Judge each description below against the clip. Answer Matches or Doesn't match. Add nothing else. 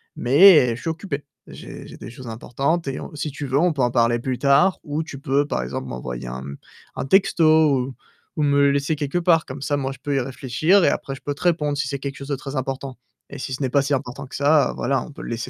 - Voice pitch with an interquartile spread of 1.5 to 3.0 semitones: Matches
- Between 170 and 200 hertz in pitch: Doesn't match